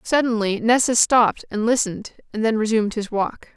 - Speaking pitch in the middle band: No, high, 225 Hz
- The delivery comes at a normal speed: Yes, average, 170 wpm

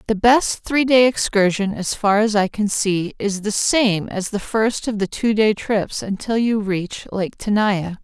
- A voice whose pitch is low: No, high, 210 Hz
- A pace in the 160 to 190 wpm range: No, average, 200 wpm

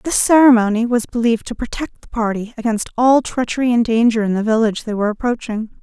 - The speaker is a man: No, female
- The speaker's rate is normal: Yes, average, 195 wpm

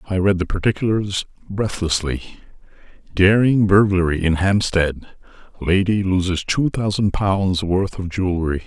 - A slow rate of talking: Yes, slow, 110 wpm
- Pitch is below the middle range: Yes, very low, 95 Hz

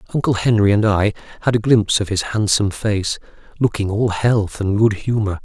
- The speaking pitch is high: No, low, 105 Hz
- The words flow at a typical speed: Yes, average, 190 wpm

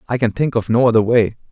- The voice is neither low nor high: No, low, 115 Hz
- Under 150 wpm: No, fast, 280 wpm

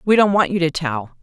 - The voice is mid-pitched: Yes, medium, 170 Hz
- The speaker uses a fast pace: Yes, fast, 295 wpm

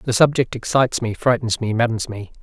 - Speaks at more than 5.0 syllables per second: Yes, 5.6 syllables/s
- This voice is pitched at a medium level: No, low, 125 Hz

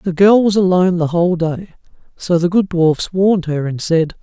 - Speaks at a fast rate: Yes, fast, 215 wpm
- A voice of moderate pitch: Yes, medium, 175 Hz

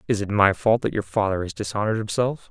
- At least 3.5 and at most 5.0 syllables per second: No, 6.4 syllables/s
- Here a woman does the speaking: No, male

